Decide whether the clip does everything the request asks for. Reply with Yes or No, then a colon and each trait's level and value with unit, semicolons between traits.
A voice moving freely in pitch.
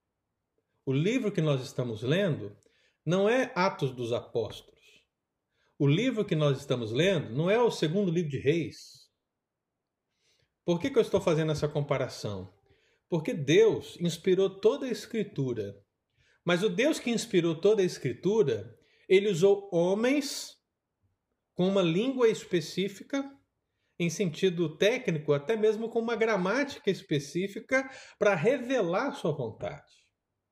Yes: wide, 7.2 semitones